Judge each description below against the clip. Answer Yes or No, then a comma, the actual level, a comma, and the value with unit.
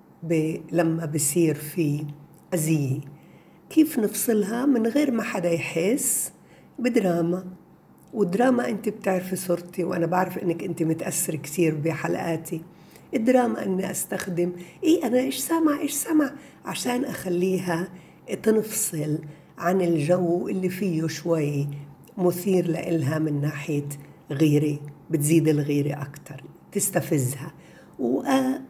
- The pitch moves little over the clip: No, average, 4.8 semitones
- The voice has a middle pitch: Yes, medium, 175 Hz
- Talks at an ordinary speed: Yes, average, 110 wpm